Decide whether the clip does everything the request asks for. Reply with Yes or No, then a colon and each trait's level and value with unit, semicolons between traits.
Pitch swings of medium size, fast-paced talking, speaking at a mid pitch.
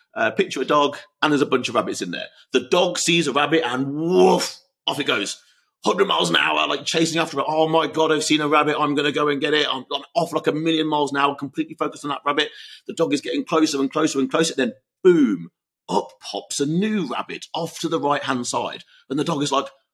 No: narrow, 2.3 semitones; fast, 260 wpm; medium, 150 Hz